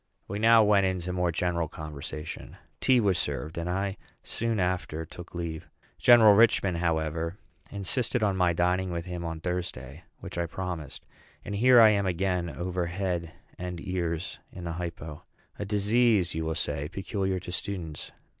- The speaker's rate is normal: Yes, average, 165 wpm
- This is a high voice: No, very low, 90 Hz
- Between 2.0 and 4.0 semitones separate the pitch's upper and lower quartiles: Yes, average, 3.0 semitones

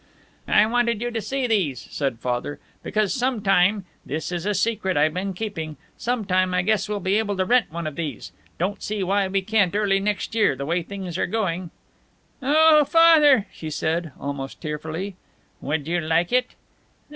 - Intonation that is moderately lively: Yes, average, 4.8 semitones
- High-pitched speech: Yes, high, 195 Hz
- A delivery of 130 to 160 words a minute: No, average, 185 wpm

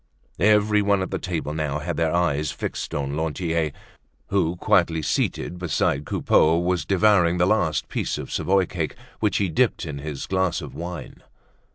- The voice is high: No, very low, 85 Hz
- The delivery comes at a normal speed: Yes, average, 165 wpm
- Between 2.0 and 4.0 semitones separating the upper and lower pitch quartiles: Yes, average, 3.4 semitones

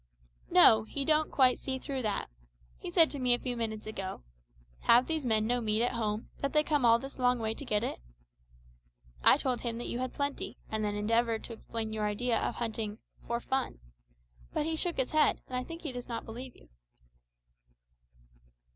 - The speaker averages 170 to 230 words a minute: Yes, average, 200 wpm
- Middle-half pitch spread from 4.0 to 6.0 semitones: No, average, 3.3 semitones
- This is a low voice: No, high, 240 Hz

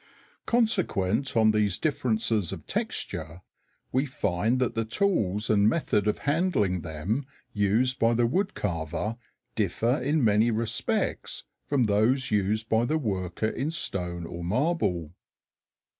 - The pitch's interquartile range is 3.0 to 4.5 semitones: No, average, 4.9 semitones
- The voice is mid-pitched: No, low, 110 Hz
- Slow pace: Yes, slow, 130 wpm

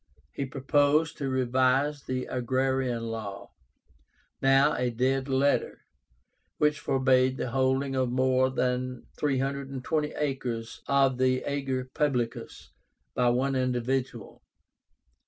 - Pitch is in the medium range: No, low, 130 Hz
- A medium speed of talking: No, slow, 105 wpm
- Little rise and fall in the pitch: Yes, narrow, 1.3 semitones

